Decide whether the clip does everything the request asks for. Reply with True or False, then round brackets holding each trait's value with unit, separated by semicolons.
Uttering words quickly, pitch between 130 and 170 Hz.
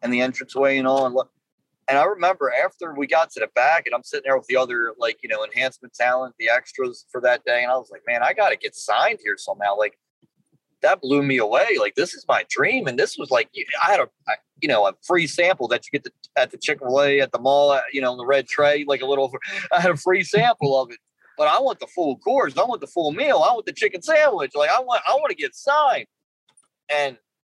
True (255 wpm; 140 Hz)